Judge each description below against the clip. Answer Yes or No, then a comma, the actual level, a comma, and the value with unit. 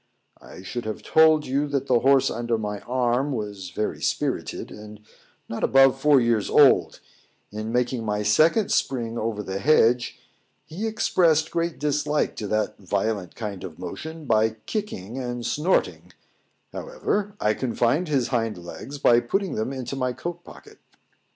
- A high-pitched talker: No, low, 125 Hz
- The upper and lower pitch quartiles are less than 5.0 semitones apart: No, wide, 5.5 semitones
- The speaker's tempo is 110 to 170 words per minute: Yes, average, 155 wpm